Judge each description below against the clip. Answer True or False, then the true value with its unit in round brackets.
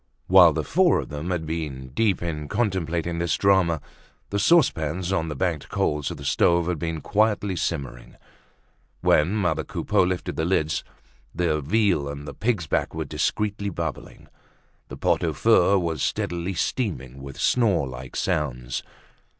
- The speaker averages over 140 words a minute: True (160 wpm)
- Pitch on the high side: False (85 Hz)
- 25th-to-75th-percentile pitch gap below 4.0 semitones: False (4.4 semitones)